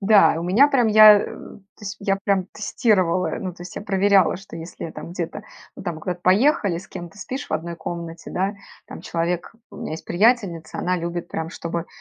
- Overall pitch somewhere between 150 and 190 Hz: Yes, medium, 185 Hz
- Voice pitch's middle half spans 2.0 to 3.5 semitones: Yes, average, 3.2 semitones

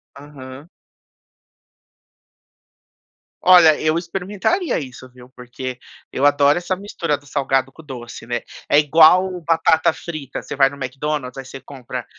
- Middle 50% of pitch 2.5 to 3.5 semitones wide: No, average, 4.1 semitones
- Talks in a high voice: No, medium, 145 Hz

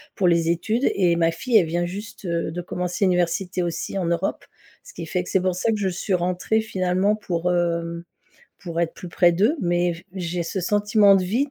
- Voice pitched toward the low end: No, medium, 180 Hz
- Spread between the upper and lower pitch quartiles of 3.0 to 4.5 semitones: No, narrow, 2.5 semitones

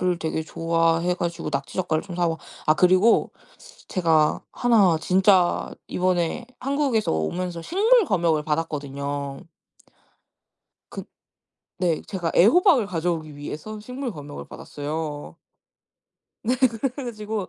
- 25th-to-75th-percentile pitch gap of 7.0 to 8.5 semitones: No, average, 5.3 semitones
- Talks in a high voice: No, medium, 175 Hz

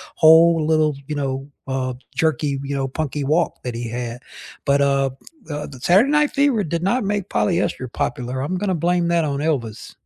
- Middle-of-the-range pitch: Yes, medium, 150 Hz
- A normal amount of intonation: Yes, average, 4.2 semitones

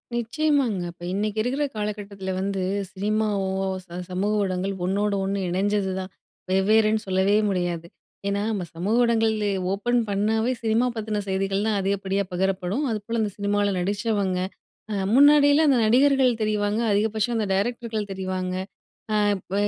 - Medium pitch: No, high, 205 Hz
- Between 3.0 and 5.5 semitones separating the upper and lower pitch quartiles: No, narrow, 2.4 semitones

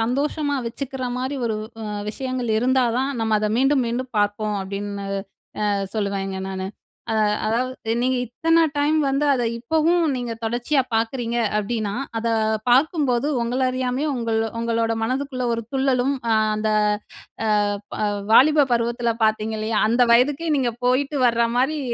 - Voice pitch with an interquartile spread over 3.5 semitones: No, average, 3.2 semitones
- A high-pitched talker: Yes, high, 245 Hz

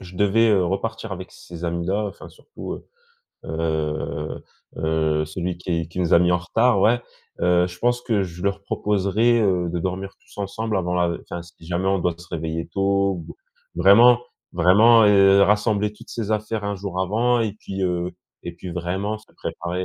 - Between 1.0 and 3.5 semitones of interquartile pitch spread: Yes, average, 3.2 semitones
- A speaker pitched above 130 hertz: No, very low, 95 Hz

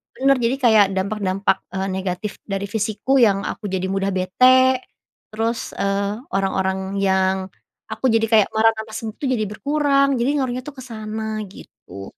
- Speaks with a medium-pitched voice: No, high, 215 Hz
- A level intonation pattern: No, average, 3.8 semitones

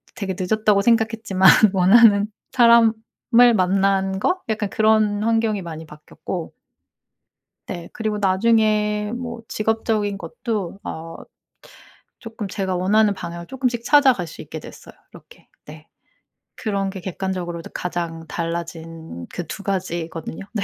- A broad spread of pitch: No, average, 3.8 semitones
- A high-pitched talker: Yes, high, 200 Hz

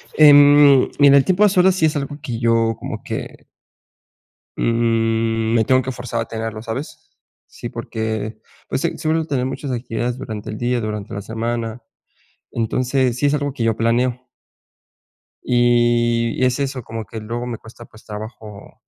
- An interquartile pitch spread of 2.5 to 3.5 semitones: Yes, average, 2.9 semitones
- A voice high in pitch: No, low, 120 Hz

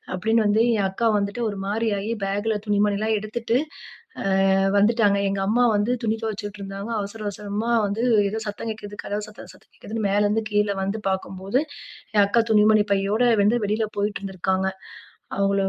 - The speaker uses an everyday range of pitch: No, narrow, 1.7 semitones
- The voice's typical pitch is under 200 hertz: No, high, 205 Hz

